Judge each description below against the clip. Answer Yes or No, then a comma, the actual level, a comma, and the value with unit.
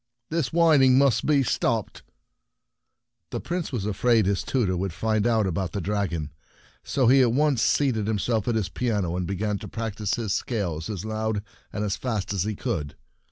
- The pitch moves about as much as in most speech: Yes, average, 4.0 semitones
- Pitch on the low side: Yes, low, 110 Hz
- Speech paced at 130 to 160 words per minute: No, average, 190 wpm